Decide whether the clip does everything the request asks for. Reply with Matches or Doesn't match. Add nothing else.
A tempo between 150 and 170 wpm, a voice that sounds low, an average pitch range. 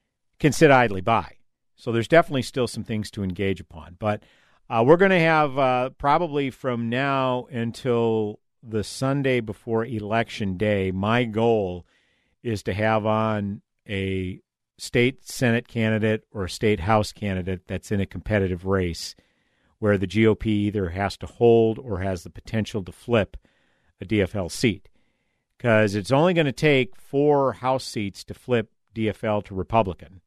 Matches